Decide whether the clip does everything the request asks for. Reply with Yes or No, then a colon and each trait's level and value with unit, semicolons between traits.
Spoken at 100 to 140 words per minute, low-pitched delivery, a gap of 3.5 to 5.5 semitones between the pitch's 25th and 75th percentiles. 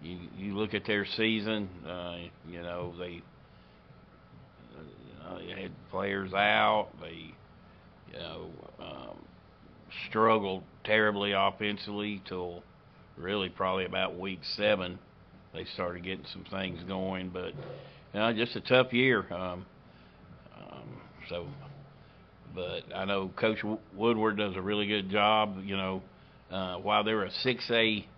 No: slow, 135 wpm; low, 100 Hz; average, 2.9 semitones